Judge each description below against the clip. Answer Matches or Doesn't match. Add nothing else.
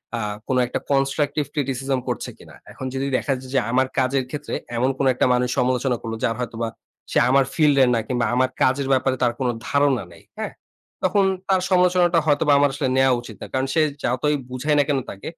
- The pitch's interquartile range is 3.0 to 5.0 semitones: Doesn't match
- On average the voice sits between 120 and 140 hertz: Matches